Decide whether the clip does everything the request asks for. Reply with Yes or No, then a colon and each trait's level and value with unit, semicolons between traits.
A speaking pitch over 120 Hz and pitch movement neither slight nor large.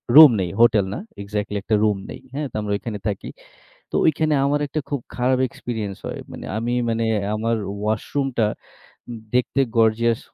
No: low, 115 Hz; average, 3.7 semitones